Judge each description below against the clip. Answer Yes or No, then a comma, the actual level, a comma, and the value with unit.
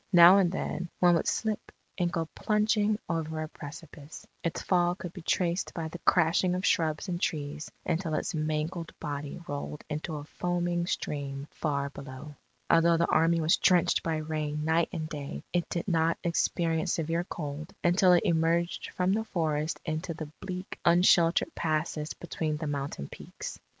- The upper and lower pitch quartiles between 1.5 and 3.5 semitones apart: Yes, narrow, 2.4 semitones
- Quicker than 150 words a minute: Yes, average, 165 wpm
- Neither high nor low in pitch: Yes, medium, 165 Hz